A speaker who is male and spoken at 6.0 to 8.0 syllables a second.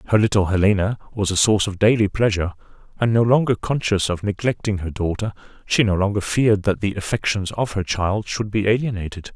Yes: male; 6.1 syllables/s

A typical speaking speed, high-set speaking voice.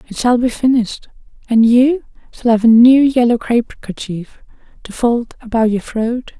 Yes: average, 170 wpm; high, 235 Hz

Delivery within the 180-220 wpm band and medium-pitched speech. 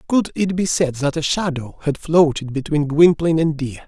Yes: average, 200 wpm; medium, 155 Hz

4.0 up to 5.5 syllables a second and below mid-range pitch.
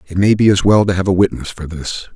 No: 6.2 syllables/s; very low, 95 Hz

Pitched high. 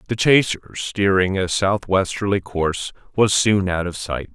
No: very low, 95 Hz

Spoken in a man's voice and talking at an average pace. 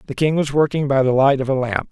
No: male; fast, 315 wpm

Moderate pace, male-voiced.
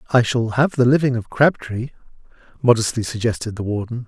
Yes: average, 160 wpm; male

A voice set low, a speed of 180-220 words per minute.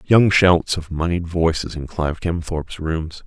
No: very low, 85 Hz; average, 165 wpm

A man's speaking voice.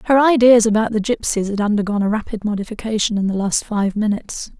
No: female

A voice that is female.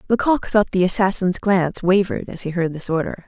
Yes: female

